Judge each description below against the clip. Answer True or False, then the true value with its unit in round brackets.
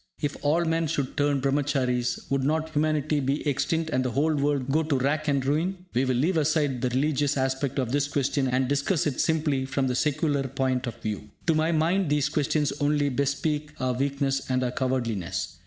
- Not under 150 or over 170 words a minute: False (200 wpm)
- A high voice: False (140 Hz)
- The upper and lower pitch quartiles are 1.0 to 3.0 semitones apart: True (2.7 semitones)